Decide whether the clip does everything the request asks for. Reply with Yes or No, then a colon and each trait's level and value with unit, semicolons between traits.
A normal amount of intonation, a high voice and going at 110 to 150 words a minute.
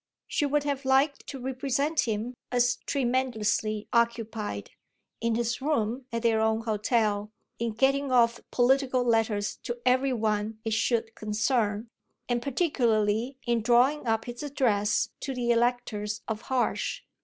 Yes: average, 3.0 semitones; high, 235 Hz; average, 140 wpm